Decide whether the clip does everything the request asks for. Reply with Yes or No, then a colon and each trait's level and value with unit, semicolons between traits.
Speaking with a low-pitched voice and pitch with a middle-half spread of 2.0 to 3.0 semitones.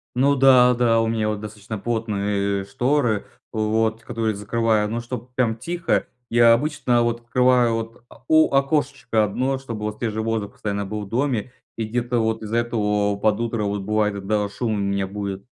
Yes: low, 115 Hz; narrow, 2.6 semitones